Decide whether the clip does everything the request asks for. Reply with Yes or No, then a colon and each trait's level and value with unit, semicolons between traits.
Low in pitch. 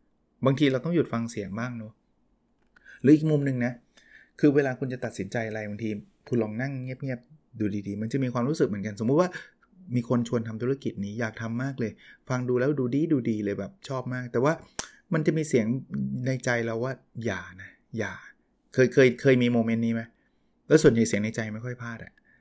Yes: low, 120 Hz